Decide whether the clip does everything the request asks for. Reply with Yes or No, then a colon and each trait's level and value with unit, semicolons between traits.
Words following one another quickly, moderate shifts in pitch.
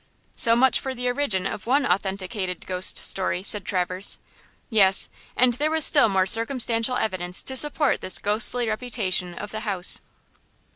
No: average, 155 wpm; average, 5.0 semitones